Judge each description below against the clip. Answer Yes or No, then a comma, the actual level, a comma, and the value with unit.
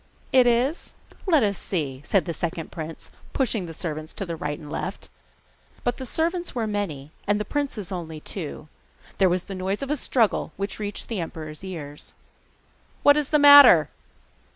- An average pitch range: No, wide, 7.4 semitones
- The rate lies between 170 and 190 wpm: Yes, average, 175 wpm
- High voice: Yes, high, 195 Hz